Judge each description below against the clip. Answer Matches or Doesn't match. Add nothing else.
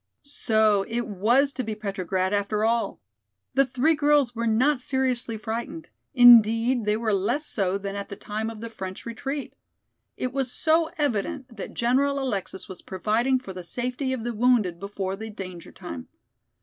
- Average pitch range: Matches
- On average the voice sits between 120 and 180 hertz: Doesn't match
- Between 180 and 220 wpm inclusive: Doesn't match